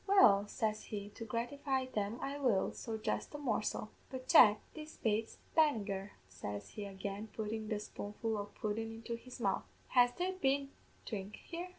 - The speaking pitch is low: No, high, 225 Hz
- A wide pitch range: No, average, 4.1 semitones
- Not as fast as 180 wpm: Yes, average, 170 wpm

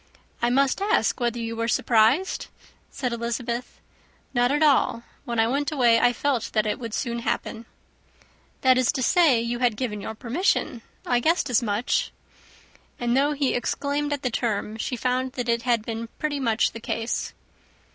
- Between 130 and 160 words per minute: No, average, 175 wpm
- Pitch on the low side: No, high, 240 Hz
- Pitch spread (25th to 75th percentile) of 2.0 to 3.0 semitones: Yes, average, 2.7 semitones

